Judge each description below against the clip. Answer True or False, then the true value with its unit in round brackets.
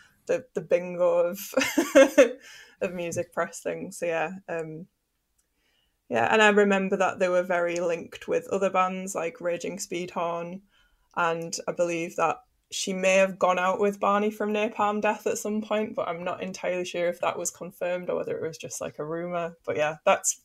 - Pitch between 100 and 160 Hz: False (185 Hz)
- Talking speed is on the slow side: False (185 wpm)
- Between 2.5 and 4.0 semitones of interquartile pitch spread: True (3.4 semitones)